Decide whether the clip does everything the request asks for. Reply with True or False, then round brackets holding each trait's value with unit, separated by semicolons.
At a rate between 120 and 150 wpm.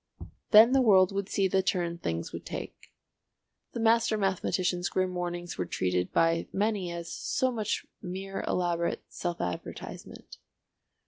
True (140 wpm)